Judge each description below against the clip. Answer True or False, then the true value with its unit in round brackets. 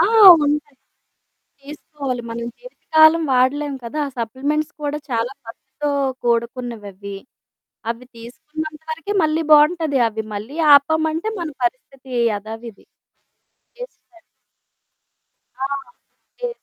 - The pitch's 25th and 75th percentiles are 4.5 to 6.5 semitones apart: True (4.9 semitones)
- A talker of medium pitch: False (280 Hz)